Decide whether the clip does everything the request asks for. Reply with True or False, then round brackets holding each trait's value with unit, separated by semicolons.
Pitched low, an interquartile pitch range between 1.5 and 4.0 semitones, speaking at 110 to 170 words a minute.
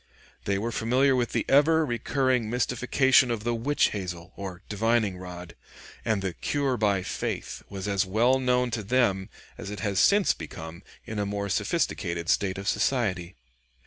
False (110 Hz; 4.5 semitones; 165 wpm)